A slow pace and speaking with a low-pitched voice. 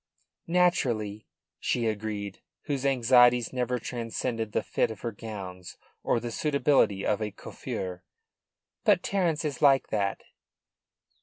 Yes: slow, 125 wpm; low, 115 Hz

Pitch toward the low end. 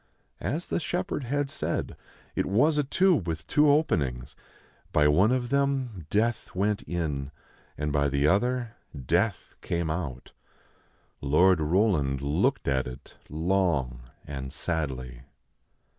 Yes: very low, 85 Hz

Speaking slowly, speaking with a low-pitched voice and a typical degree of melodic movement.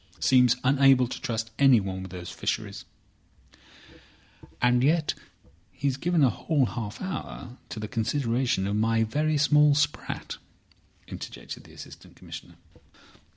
Yes: slow, 125 wpm; low, 125 Hz; average, 4.4 semitones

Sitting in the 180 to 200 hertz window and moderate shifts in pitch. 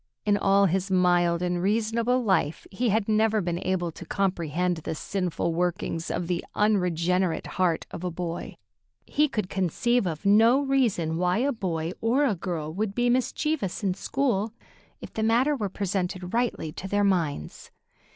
Yes: high, 190 Hz; average, 4.1 semitones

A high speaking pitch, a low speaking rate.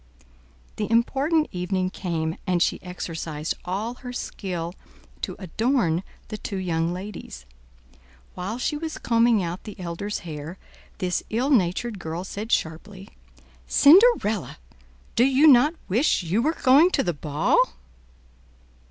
Yes: high, 195 Hz; slow, 130 wpm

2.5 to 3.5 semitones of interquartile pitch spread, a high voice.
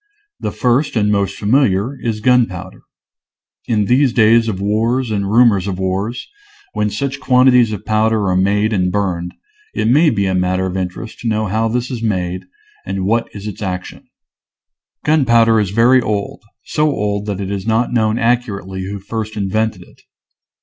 No: average, 3.2 semitones; low, 110 Hz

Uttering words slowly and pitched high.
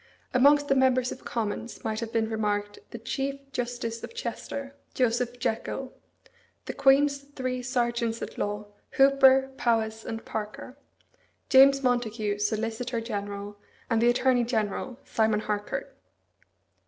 Yes: slow, 130 wpm; high, 235 Hz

